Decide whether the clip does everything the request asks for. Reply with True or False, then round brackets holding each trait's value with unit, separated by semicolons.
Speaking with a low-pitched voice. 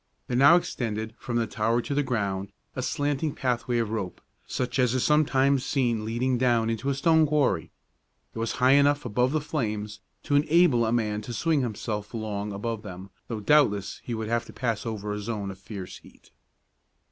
True (120 Hz)